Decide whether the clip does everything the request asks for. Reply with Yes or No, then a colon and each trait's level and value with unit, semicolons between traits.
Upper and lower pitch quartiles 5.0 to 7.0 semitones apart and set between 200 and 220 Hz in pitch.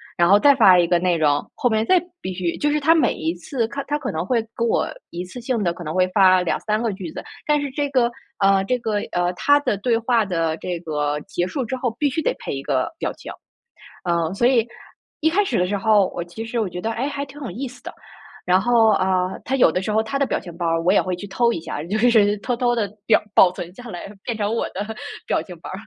Yes: wide, 5.5 semitones; high, 205 Hz